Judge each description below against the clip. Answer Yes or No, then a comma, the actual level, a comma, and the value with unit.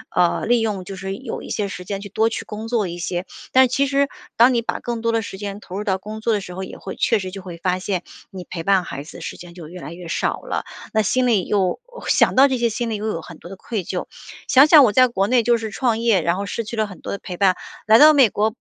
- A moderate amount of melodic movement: Yes, average, 4.0 semitones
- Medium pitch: No, high, 205 Hz